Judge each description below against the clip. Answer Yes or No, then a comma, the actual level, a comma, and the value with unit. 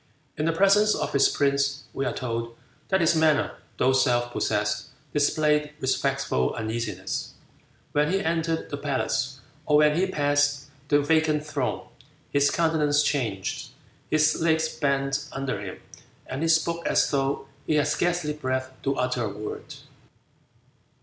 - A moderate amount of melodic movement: Yes, average, 3.3 semitones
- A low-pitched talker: No, medium, 145 Hz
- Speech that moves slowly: No, average, 145 wpm